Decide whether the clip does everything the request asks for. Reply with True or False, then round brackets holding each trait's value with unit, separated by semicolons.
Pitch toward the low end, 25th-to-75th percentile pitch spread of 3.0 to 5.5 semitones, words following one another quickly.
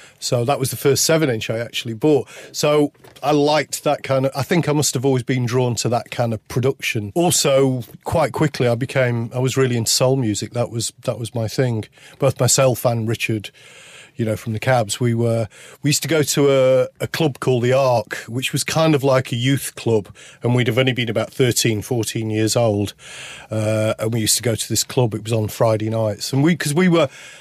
True (125 Hz; 3.5 semitones; 230 wpm)